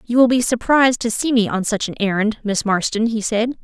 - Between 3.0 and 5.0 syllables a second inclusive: No, 5.6 syllables/s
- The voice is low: No, high, 225 Hz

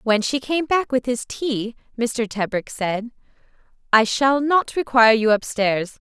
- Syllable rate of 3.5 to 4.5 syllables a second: Yes, 4.2 syllables/s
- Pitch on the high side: Yes, high, 240 Hz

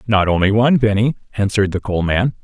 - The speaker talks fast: No, average, 195 wpm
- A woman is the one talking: No, male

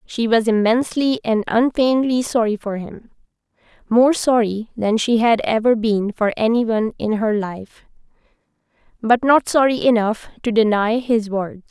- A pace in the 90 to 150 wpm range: Yes, average, 145 wpm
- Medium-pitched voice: No, high, 230 Hz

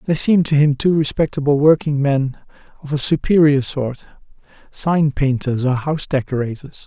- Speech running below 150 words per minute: Yes, average, 140 wpm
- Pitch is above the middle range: No, medium, 145 Hz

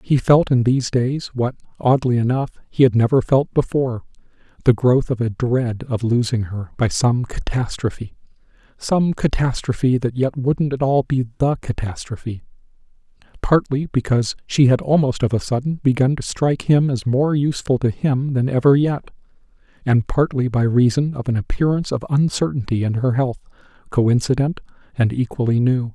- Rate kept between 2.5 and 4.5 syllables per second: No, 5.1 syllables/s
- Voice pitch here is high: No, low, 130 Hz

